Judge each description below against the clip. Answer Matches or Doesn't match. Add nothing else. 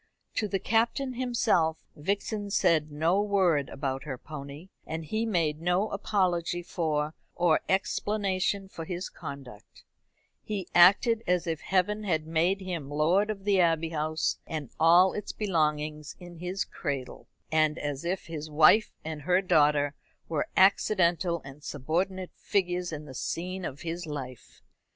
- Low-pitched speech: Doesn't match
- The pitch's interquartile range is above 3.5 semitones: Matches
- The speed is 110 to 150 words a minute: Matches